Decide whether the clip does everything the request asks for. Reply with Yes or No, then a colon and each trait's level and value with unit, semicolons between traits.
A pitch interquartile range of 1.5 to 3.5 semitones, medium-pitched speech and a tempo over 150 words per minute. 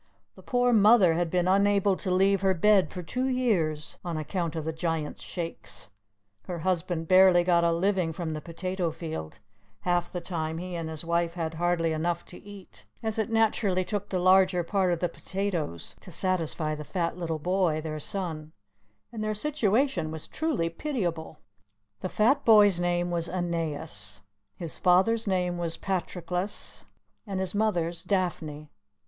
Yes: average, 3.0 semitones; medium, 175 Hz; average, 165 wpm